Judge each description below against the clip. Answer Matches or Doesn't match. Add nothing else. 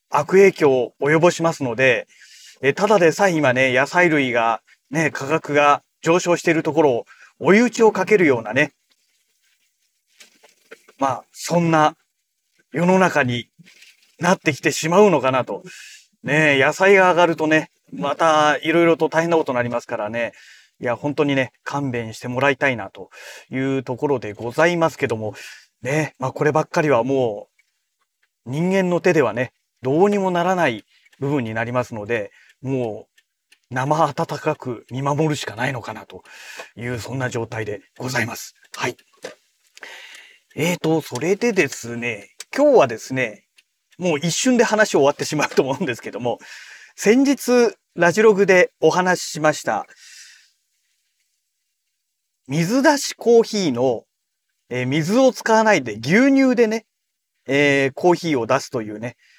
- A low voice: Doesn't match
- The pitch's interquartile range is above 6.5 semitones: Doesn't match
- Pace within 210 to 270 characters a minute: Doesn't match